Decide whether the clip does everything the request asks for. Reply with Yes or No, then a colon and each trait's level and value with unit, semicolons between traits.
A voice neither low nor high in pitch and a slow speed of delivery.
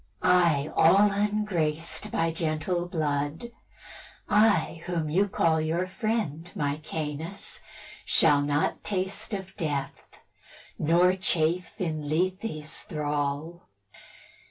Yes: medium, 165 Hz; slow, 95 wpm